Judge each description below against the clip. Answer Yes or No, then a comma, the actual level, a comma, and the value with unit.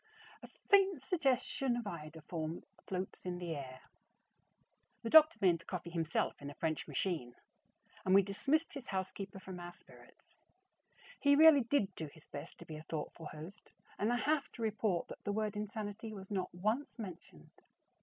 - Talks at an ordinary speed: Yes, average, 170 wpm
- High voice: Yes, high, 195 Hz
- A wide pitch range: Yes, wide, 6.0 semitones